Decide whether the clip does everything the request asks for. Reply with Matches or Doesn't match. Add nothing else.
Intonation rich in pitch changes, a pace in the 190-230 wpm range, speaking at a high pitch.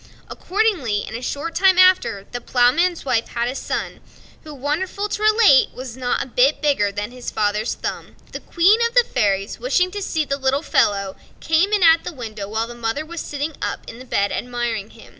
Matches